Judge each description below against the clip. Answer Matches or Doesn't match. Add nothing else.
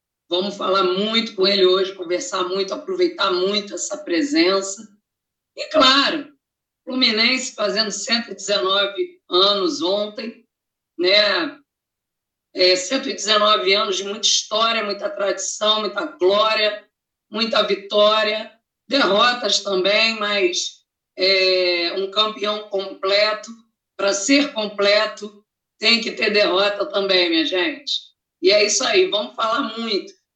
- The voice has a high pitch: Matches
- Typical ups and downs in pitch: Matches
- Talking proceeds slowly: Matches